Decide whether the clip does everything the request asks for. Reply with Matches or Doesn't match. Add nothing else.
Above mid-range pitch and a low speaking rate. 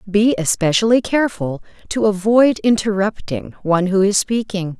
Matches